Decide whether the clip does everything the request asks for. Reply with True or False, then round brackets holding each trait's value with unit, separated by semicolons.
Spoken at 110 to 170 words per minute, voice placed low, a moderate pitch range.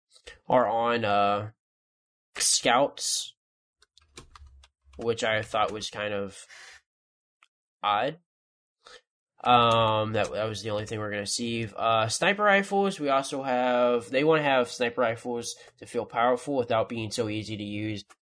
True (140 wpm; 115 Hz; 3.1 semitones)